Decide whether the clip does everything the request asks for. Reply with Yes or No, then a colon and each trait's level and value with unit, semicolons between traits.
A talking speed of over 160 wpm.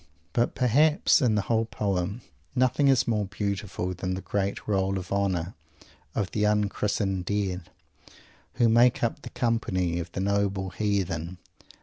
No: average, 145 wpm